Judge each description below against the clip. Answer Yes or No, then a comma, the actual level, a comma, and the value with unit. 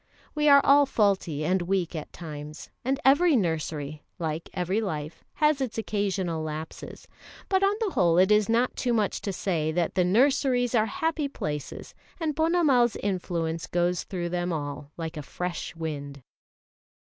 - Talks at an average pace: Yes, average, 160 wpm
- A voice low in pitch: No, medium, 185 Hz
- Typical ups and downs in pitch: No, wide, 7.7 semitones